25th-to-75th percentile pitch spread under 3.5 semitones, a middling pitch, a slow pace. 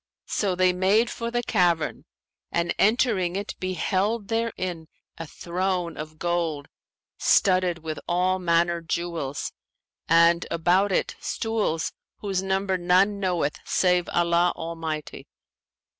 Yes: narrow, 2.4 semitones; medium, 180 Hz; slow, 115 wpm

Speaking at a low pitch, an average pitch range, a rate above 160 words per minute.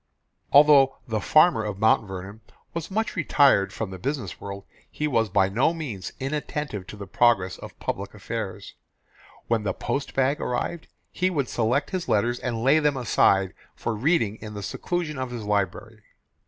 No: low, 120 Hz; wide, 6.2 semitones; average, 170 wpm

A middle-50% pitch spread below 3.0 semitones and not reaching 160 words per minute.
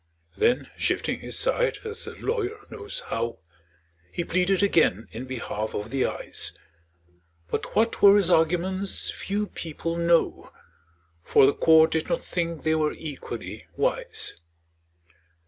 No: average, 5.0 semitones; slow, 135 wpm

